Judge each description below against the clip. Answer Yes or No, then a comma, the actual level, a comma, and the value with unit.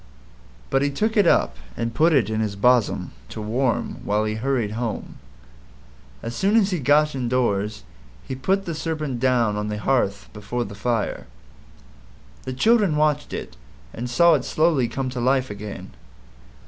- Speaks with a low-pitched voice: Yes, low, 125 Hz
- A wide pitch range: Yes, wide, 5.7 semitones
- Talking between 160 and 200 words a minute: Yes, average, 165 wpm